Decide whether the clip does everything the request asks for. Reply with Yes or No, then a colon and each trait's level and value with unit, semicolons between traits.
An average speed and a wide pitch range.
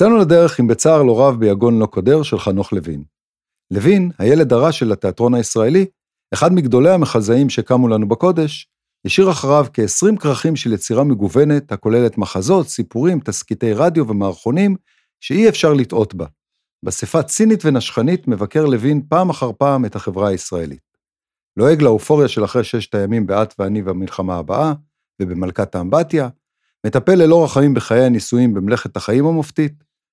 Yes: average, 135 wpm; wide, 6.6 semitones